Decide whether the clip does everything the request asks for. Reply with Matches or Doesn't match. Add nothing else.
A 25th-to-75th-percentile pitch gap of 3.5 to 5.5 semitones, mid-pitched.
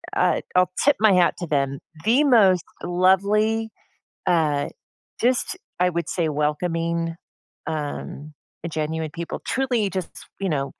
Matches